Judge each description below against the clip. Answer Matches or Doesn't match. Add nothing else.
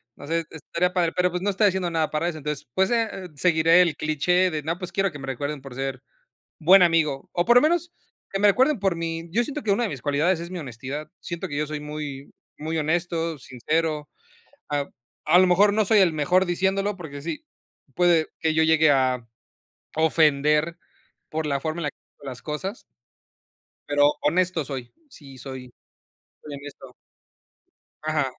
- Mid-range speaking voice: Matches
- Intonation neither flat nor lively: Matches